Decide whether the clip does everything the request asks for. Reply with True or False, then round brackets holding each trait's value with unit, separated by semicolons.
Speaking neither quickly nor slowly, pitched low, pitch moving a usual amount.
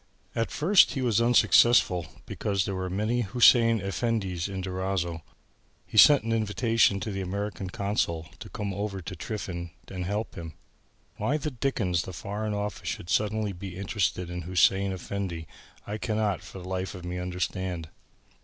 True (165 wpm; 100 Hz; 3.0 semitones)